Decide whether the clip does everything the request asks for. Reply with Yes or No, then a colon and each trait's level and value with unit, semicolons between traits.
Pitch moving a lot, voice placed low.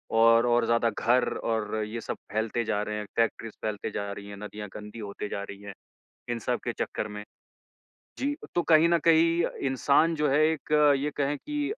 Yes: wide, 6.1 semitones; low, 115 Hz